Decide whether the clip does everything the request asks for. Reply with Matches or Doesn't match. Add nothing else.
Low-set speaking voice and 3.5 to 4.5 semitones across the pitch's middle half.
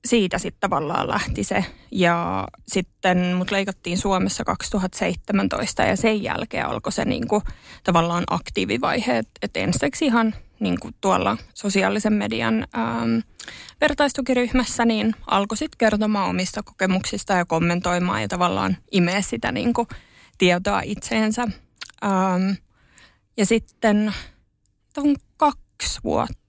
Doesn't match